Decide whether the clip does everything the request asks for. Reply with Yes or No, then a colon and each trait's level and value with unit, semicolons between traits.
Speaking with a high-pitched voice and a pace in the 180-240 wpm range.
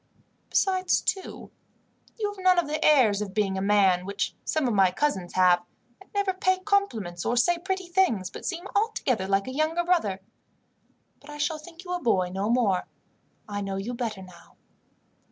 Yes: very high, 250 Hz; average, 185 wpm